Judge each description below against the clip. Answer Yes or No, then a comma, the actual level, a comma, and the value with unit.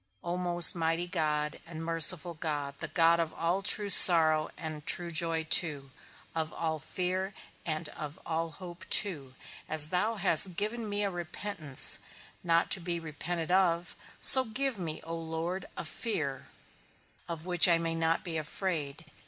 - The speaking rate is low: No, average, 160 wpm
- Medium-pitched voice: Yes, medium, 165 Hz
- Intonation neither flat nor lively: No, narrow, 2.3 semitones